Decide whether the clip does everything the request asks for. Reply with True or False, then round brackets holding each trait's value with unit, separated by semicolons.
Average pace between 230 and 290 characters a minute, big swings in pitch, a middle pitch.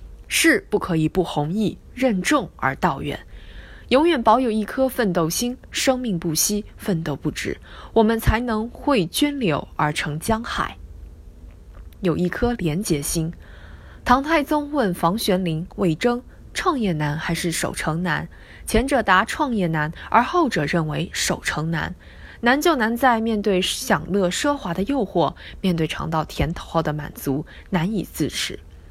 False (215 characters per minute; 7.1 semitones; 180 Hz)